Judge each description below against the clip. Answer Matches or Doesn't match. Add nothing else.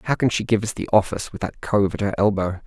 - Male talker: Matches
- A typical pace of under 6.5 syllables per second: Doesn't match